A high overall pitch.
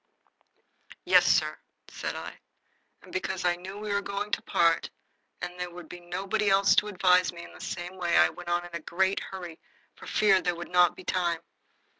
No: medium, 180 Hz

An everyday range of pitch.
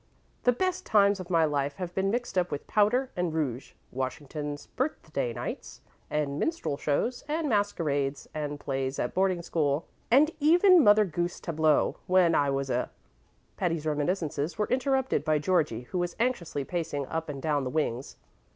No: wide, 6.1 semitones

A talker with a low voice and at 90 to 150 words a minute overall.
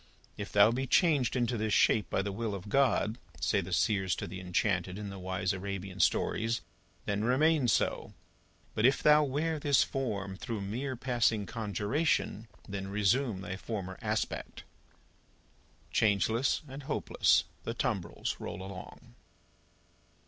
Yes: low, 105 Hz; average, 140 wpm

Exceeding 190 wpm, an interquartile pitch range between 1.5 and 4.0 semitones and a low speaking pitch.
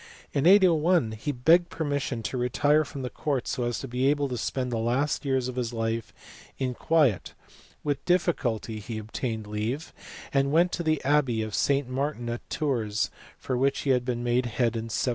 Yes: average, 200 wpm; average, 3.7 semitones; low, 130 Hz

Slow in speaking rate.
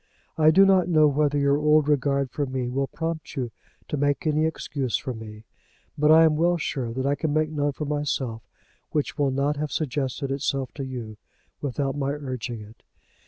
No: average, 195 wpm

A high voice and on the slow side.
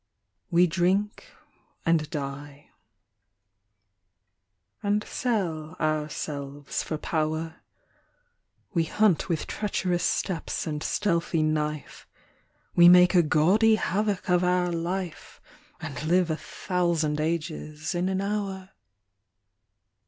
No: medium, 170 Hz; slow, 95 wpm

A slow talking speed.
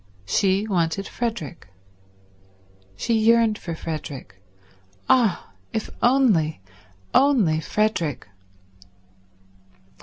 Yes: slow, 70 wpm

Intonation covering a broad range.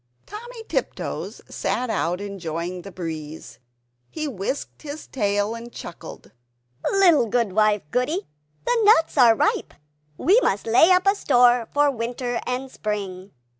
Yes: wide, 6.9 semitones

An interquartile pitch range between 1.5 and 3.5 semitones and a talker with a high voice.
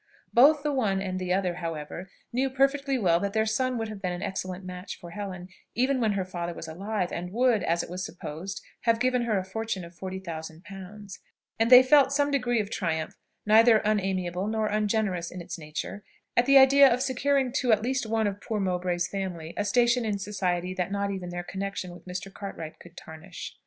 No: average, 4.6 semitones; high, 200 Hz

